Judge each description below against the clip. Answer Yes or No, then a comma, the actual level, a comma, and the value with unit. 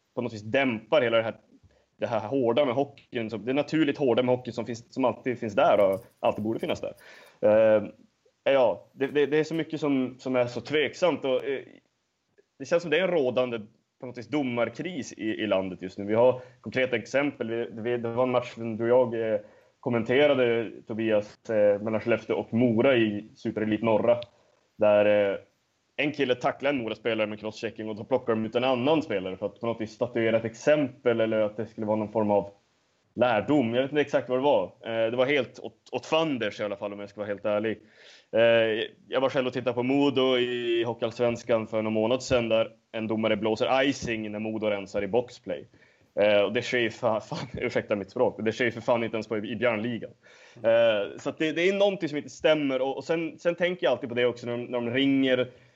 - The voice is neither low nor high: No, low, 120 Hz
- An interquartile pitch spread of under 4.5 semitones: Yes, average, 3.0 semitones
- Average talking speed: No, fast, 210 wpm